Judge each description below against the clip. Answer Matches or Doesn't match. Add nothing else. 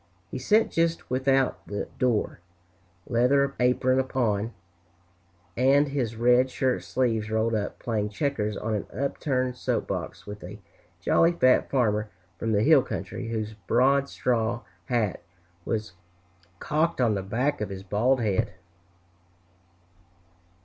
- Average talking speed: Doesn't match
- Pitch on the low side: Matches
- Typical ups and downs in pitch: Matches